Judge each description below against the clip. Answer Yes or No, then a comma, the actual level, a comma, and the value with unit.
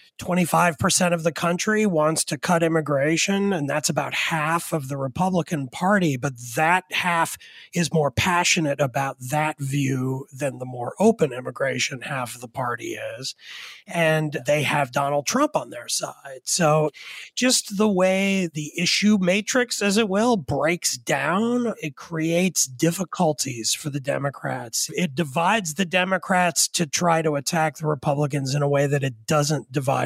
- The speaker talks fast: No, average, 155 wpm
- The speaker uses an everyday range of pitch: Yes, average, 4.1 semitones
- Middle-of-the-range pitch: Yes, medium, 160 Hz